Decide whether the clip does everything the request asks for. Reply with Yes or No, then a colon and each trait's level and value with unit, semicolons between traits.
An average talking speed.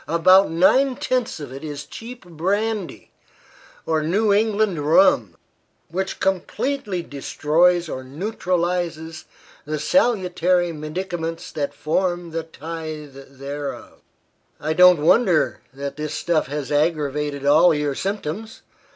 No: slow, 115 wpm